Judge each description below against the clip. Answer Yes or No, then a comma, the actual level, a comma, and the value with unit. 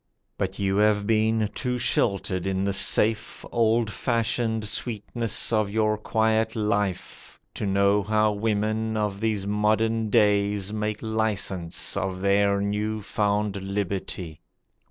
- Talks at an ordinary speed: No, slow, 125 wpm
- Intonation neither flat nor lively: No, narrow, 1.8 semitones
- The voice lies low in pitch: Yes, low, 105 Hz